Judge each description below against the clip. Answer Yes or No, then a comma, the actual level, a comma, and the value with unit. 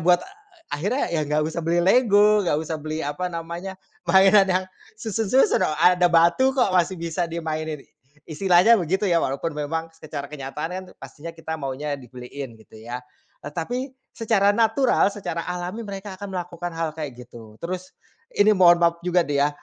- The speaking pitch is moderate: Yes, medium, 170 Hz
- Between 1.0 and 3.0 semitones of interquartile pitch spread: No, average, 3.7 semitones